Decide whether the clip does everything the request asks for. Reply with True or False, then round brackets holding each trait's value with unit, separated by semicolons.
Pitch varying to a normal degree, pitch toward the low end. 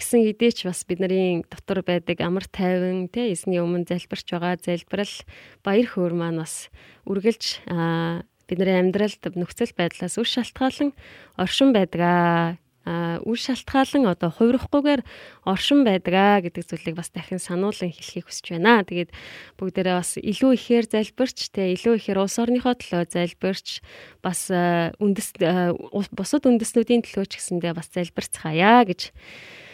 False (4.6 semitones; 185 Hz)